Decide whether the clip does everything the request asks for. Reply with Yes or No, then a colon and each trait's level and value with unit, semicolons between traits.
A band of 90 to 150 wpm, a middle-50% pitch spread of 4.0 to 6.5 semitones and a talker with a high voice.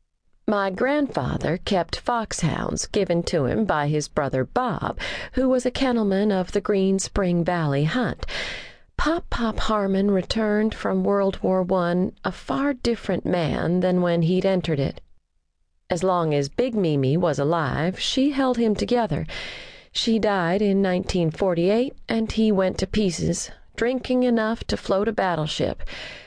Yes: average, 145 wpm; average, 4.6 semitones; high, 195 Hz